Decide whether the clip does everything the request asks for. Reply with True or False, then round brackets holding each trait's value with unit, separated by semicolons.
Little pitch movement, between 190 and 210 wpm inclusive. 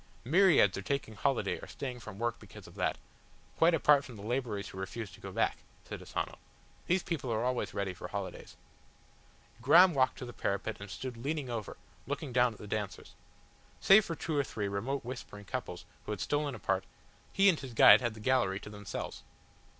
False (5.4 semitones; 195 wpm)